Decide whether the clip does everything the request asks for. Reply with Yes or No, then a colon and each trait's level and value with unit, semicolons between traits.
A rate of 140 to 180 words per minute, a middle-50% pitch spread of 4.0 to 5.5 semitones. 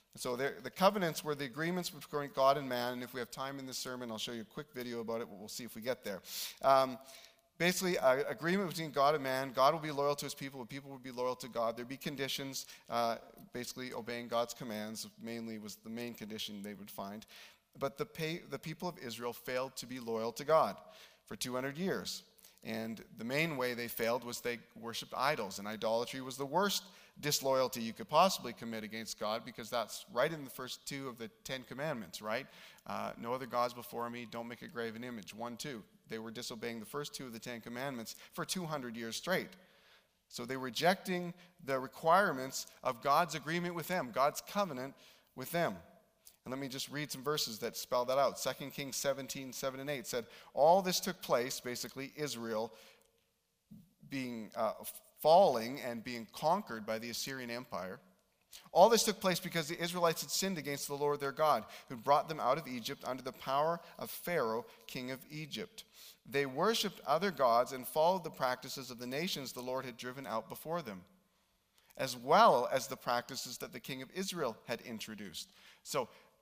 No: average, 200 wpm; average, 4.3 semitones